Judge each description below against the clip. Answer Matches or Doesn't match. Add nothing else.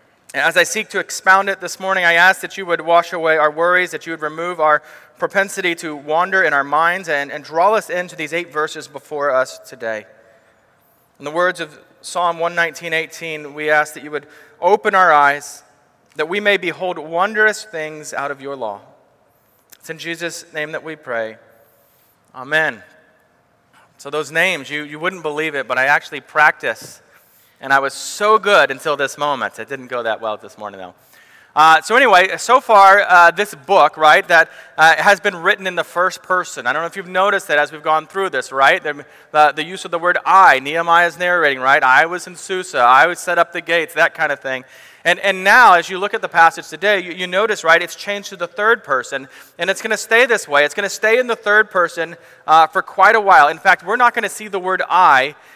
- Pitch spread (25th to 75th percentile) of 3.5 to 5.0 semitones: Matches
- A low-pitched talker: Doesn't match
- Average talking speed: Doesn't match